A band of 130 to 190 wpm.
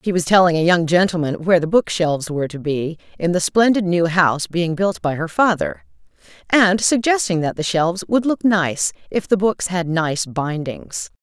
No: average, 200 wpm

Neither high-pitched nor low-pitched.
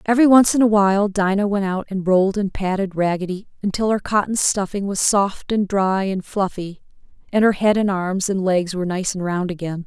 No: high, 195 Hz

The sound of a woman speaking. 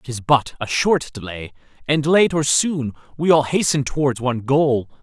No: male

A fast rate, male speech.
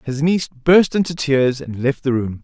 Yes: fast, 220 wpm; male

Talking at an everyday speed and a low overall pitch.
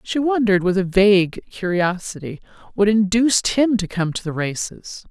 No: average, 165 wpm; high, 200 Hz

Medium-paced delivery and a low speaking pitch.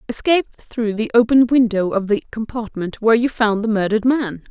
No: average, 185 wpm; high, 225 Hz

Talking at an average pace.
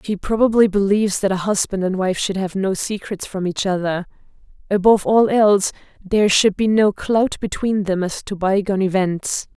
Yes: average, 180 wpm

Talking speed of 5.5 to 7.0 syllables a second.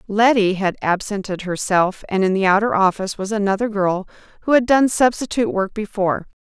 Yes: 5.7 syllables/s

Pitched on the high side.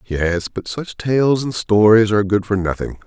No: low, 105 Hz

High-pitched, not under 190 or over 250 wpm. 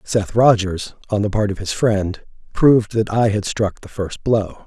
No: low, 105 Hz; fast, 205 wpm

